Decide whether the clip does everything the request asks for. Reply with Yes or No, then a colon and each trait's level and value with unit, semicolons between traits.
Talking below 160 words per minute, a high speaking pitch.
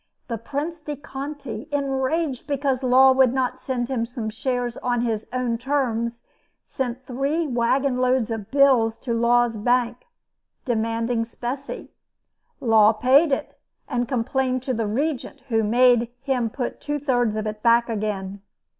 Yes: average, 145 wpm; high, 245 Hz